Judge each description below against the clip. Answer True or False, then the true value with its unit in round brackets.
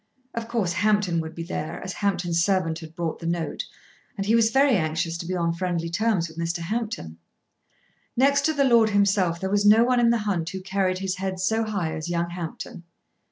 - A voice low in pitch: False (185 Hz)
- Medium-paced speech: False (210 wpm)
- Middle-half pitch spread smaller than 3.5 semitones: False (4.2 semitones)